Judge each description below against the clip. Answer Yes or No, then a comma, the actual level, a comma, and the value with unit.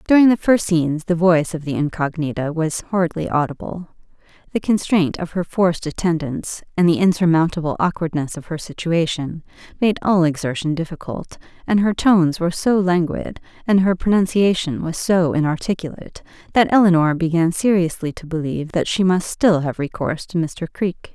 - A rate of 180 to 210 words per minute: No, average, 160 wpm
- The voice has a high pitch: No, medium, 170 Hz